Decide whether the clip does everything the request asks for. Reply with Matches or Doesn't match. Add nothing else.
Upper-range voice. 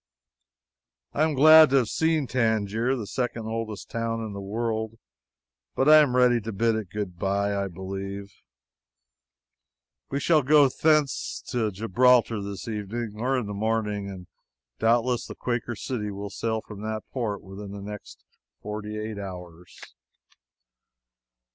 Doesn't match